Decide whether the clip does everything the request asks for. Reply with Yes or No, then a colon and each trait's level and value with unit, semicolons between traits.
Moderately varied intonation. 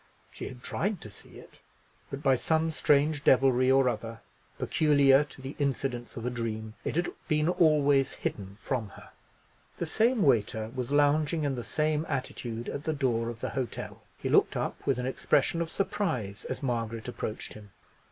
Yes: average, 4.5 semitones